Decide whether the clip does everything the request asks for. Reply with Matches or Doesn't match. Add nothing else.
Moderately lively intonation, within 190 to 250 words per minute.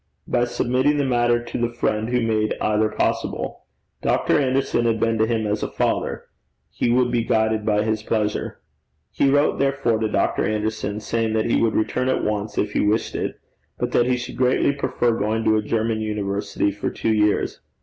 Doesn't match